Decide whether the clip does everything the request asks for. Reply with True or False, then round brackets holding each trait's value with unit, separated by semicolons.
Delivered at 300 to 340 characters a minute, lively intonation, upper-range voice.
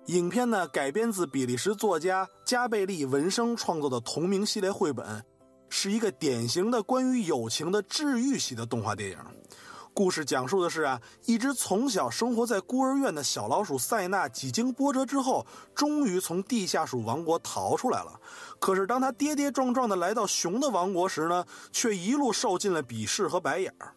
False (285 characters per minute; 8.4 semitones; 195 Hz)